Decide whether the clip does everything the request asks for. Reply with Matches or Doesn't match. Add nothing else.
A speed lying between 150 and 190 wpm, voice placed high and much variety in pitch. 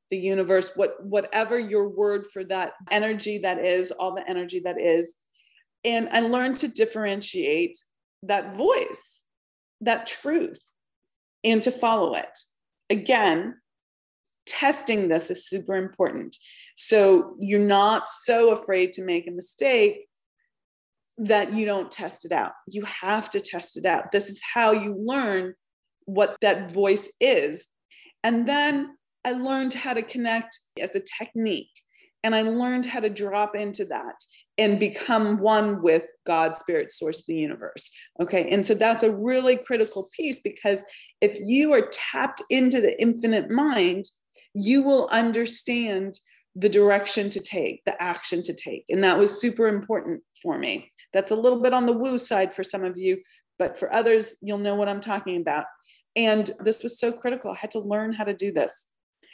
Doesn't match